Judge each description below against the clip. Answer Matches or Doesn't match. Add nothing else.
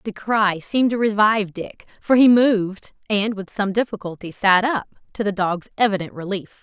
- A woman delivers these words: Matches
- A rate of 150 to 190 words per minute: Matches